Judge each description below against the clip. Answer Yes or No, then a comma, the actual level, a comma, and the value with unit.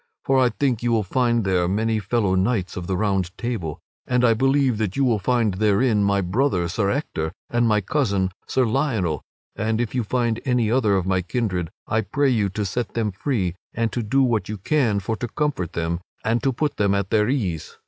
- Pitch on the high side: No, low, 110 Hz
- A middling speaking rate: No, fast, 215 wpm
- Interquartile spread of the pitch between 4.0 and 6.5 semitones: Yes, average, 4.3 semitones